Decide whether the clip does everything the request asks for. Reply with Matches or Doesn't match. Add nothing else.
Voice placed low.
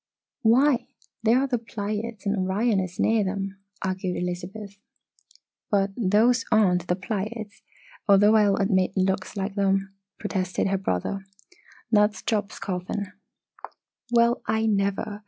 Doesn't match